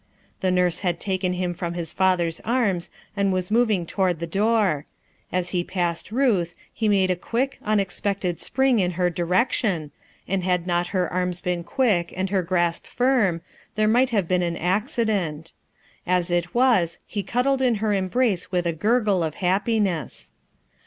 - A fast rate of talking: No, average, 170 wpm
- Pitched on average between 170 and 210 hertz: Yes, medium, 185 Hz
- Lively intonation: No, average, 3.5 semitones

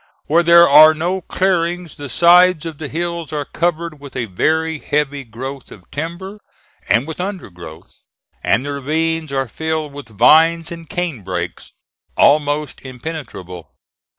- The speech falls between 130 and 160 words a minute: Yes, average, 140 wpm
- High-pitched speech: No, medium, 155 Hz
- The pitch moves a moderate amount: Yes, average, 3.9 semitones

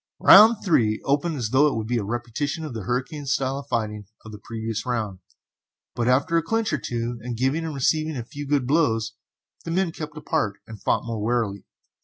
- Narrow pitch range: No, average, 5.2 semitones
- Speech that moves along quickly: Yes, fast, 210 wpm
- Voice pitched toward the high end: No, low, 125 Hz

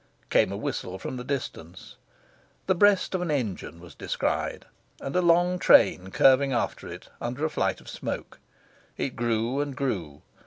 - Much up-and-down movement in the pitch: Yes, wide, 6.8 semitones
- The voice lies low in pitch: Yes, low, 130 Hz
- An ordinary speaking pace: Yes, average, 165 wpm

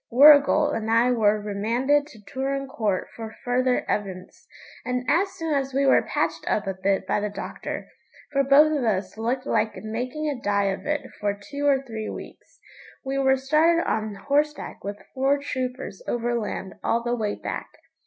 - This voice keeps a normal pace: Yes, average, 175 wpm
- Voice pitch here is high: Yes, very high, 250 Hz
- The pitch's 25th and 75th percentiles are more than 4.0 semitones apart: Yes, average, 4.8 semitones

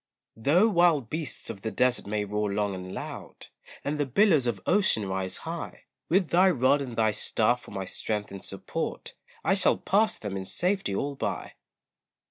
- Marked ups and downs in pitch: Yes, wide, 8.7 semitones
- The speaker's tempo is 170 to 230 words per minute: Yes, average, 180 wpm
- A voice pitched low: Yes, low, 125 Hz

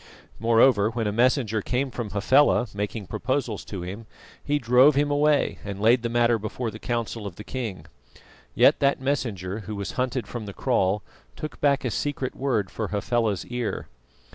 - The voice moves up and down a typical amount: Yes, average, 3.8 semitones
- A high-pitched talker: No, low, 115 Hz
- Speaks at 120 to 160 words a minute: No, average, 175 wpm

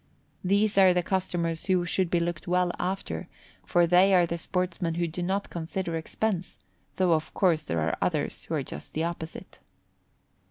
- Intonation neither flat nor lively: No, narrow, 1.9 semitones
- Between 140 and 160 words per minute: No, average, 175 wpm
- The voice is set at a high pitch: No, medium, 175 Hz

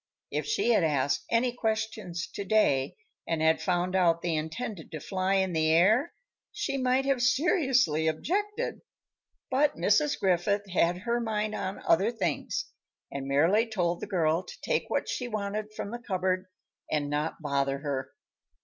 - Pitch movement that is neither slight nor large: No, wide, 6.3 semitones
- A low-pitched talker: No, high, 190 Hz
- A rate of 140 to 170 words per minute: Yes, average, 160 wpm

